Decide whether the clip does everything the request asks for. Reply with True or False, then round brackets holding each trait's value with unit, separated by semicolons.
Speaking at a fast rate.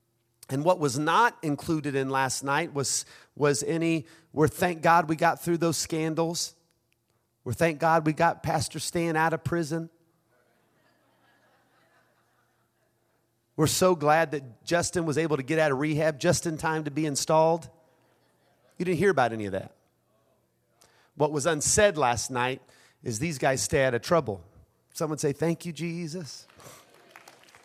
False (155 wpm)